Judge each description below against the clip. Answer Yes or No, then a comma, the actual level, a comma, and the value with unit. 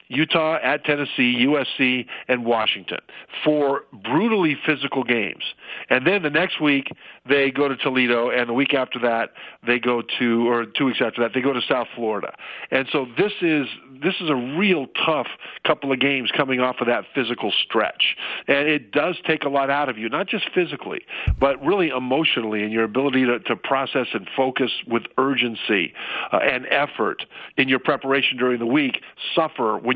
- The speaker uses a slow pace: No, average, 180 wpm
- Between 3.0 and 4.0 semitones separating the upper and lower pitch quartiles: Yes, average, 3.3 semitones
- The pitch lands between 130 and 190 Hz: Yes, low, 135 Hz